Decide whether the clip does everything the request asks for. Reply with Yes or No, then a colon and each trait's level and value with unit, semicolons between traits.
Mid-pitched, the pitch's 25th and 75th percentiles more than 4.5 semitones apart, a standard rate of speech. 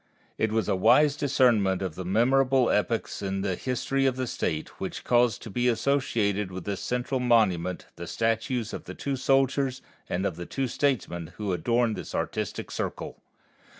No: low, 115 Hz; average, 5.2 semitones; average, 170 wpm